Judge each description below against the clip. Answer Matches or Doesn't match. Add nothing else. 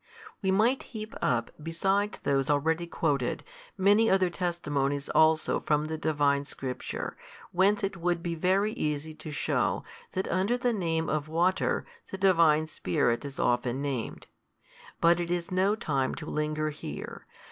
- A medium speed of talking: Matches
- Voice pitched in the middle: Matches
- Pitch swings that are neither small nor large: Matches